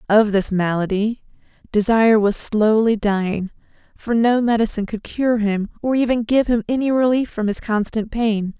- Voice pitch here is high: Yes, high, 220 Hz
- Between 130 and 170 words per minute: Yes, average, 160 wpm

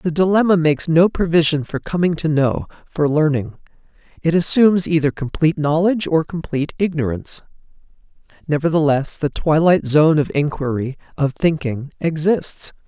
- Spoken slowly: Yes, slow, 130 wpm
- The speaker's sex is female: No, male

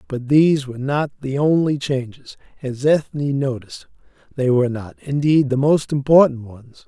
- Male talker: Yes, male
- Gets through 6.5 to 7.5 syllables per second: No, 5.0 syllables/s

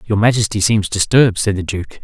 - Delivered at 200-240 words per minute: Yes, fast, 205 wpm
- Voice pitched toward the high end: No, low, 105 Hz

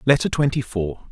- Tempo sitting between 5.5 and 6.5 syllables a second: No, 5.2 syllables/s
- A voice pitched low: Yes, low, 120 Hz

